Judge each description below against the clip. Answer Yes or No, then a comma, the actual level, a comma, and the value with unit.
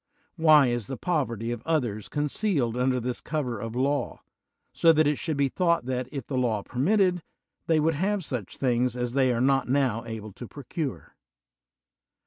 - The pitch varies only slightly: No, average, 4.3 semitones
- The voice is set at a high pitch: No, low, 130 Hz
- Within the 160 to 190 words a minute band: Yes, average, 175 wpm